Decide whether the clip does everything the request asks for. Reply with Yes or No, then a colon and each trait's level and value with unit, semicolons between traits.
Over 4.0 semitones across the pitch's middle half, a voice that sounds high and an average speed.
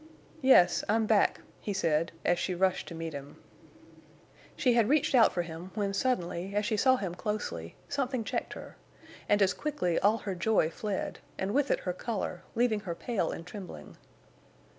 Yes: average, 4.5 semitones; high, 200 Hz; average, 180 wpm